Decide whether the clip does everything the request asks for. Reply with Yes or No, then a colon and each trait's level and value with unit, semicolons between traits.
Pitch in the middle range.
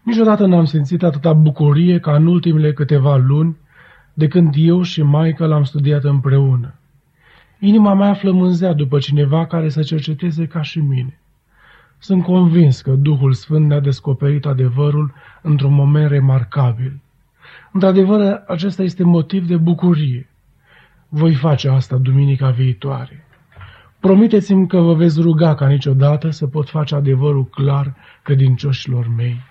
Yes: medium, 150 Hz